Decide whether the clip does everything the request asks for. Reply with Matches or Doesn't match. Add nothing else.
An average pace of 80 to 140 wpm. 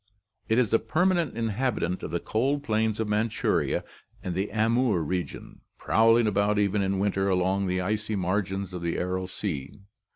Doesn't match